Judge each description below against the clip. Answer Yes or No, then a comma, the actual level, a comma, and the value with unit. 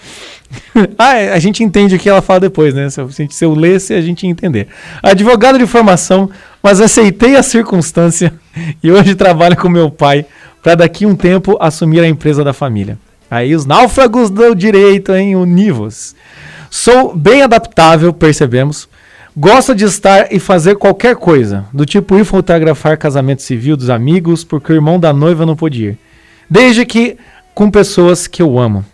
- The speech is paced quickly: No, average, 175 wpm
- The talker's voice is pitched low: No, medium, 175 Hz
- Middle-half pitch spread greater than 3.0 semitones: Yes, average, 4.6 semitones